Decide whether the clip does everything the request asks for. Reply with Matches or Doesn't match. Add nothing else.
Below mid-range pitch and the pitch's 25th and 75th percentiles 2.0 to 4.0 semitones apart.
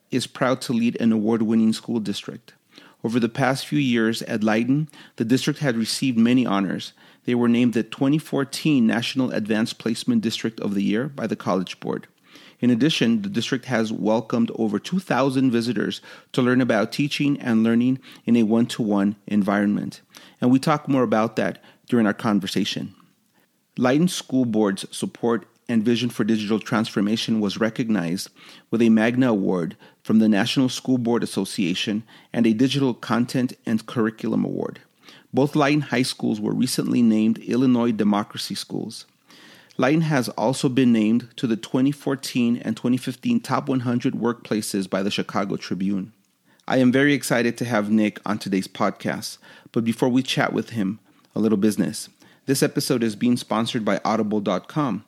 Matches